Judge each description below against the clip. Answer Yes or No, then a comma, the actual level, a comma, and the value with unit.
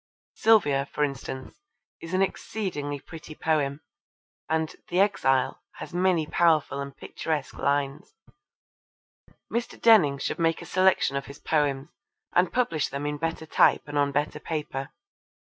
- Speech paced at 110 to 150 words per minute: Yes, average, 140 wpm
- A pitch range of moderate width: Yes, average, 3.6 semitones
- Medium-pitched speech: Yes, medium, 150 Hz